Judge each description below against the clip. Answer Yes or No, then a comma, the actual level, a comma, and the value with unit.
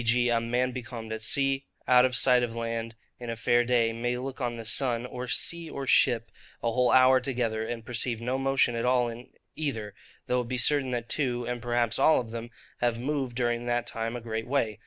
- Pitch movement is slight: Yes, narrow, 1.6 semitones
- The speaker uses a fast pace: Yes, fast, 220 wpm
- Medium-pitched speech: No, low, 120 Hz